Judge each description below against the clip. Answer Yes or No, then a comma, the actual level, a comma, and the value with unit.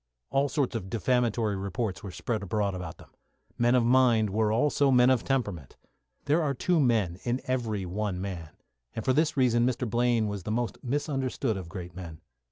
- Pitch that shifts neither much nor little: Yes, average, 4.5 semitones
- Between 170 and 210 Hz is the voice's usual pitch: No, low, 115 Hz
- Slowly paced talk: No, average, 185 wpm